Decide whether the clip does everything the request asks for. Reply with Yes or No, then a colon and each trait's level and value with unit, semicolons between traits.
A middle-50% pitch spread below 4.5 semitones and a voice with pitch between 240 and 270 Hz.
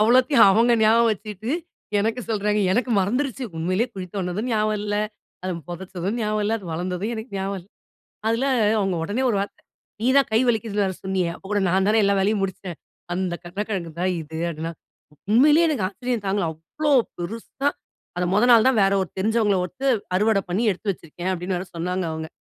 No: average, 3.4 semitones; high, 205 Hz